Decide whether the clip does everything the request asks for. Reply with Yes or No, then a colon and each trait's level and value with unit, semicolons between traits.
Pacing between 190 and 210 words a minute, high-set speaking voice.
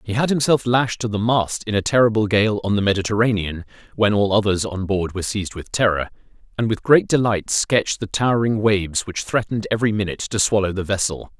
No: fast, 205 wpm; low, 105 Hz